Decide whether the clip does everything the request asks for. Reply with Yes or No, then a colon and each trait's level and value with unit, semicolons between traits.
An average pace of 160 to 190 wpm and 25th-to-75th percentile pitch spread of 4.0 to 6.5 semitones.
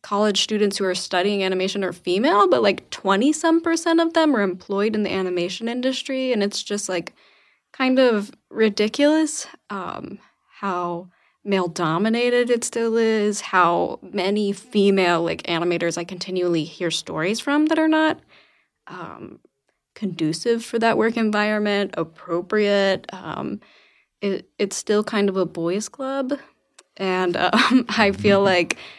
No: average, 145 wpm; average, 4.5 semitones